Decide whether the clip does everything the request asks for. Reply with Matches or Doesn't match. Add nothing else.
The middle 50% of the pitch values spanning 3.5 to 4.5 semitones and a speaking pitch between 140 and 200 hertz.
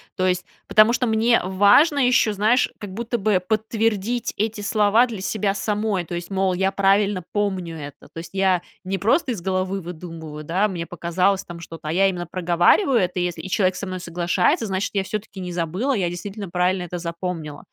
Doesn't match